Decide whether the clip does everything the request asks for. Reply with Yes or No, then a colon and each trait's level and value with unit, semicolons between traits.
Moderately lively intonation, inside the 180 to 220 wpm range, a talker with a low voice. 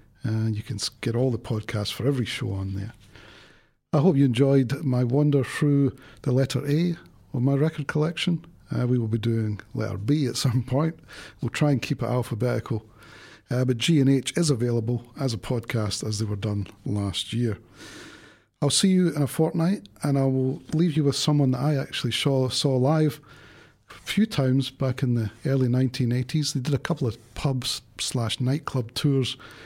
Yes: average, 3.8 semitones; average, 190 wpm; low, 130 Hz